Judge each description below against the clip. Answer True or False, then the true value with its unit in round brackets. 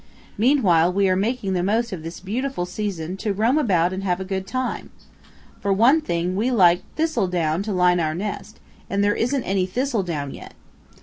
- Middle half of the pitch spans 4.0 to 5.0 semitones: True (4.3 semitones)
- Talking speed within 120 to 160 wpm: False (185 wpm)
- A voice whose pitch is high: True (195 Hz)